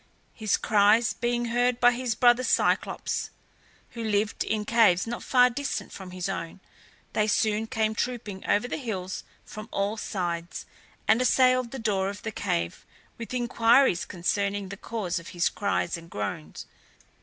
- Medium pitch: No, high, 215 Hz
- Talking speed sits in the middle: Yes, average, 155 wpm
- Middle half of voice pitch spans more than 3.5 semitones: Yes, average, 3.9 semitones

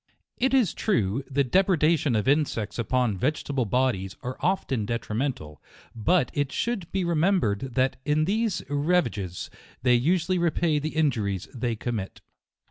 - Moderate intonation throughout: No, wide, 6.7 semitones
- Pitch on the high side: No, low, 135 Hz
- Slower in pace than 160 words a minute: Yes, average, 140 wpm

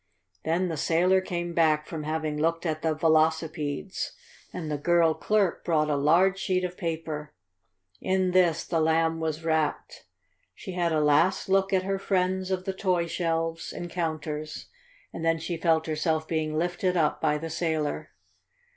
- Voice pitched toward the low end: No, medium, 165 Hz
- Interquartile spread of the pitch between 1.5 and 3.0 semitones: Yes, narrow, 2.5 semitones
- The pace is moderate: Yes, average, 165 wpm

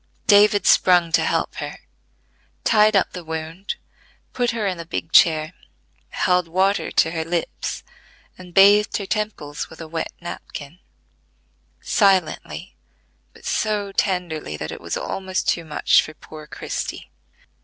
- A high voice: No, medium, 180 Hz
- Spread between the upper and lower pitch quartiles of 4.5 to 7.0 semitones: No, average, 3.8 semitones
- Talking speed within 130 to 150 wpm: Yes, average, 140 wpm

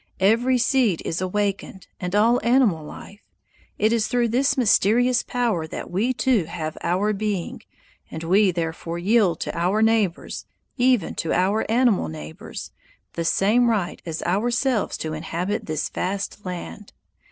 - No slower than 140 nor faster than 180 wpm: Yes, average, 145 wpm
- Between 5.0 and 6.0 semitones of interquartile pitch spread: Yes, average, 5.3 semitones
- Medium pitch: No, high, 205 Hz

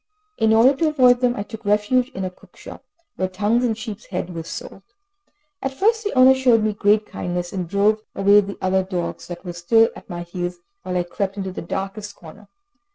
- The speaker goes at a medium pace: No, fast, 210 wpm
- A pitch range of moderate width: Yes, average, 3.8 semitones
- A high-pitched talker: Yes, high, 205 Hz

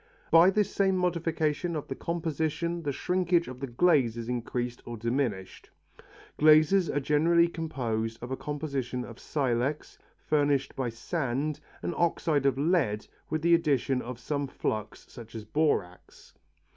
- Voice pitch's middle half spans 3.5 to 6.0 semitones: Yes, average, 5.2 semitones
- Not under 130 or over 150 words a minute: Yes, average, 145 wpm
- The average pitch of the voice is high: No, medium, 145 Hz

